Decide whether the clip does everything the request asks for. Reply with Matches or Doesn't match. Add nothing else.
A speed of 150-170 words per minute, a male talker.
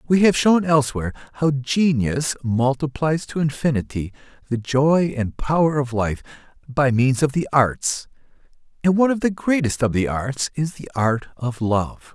Matches